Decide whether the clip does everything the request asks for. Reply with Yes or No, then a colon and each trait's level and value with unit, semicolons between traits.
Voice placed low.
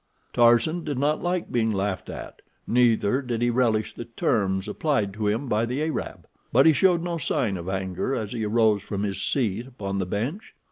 Yes: low, 115 Hz